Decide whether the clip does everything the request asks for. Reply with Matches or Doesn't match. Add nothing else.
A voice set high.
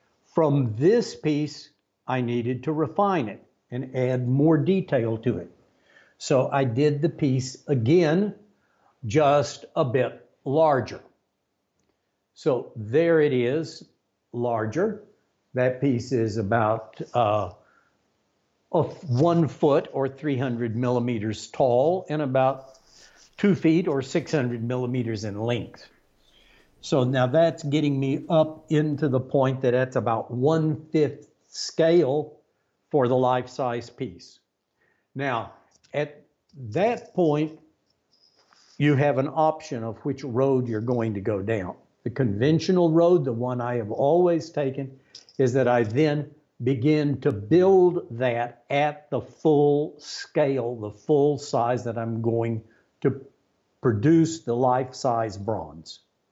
Doesn't match